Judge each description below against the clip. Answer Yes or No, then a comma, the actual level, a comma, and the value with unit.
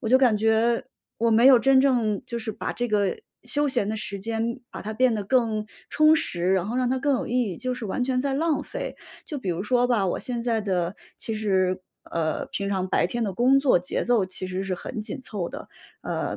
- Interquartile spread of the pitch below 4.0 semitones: No, average, 4.3 semitones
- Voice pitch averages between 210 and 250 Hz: Yes, high, 225 Hz